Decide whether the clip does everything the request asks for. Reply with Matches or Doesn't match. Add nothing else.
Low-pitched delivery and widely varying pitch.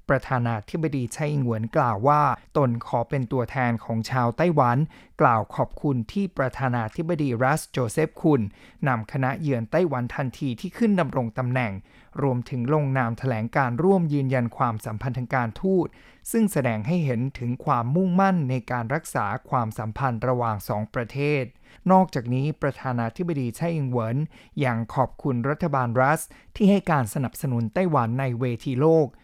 Doesn't match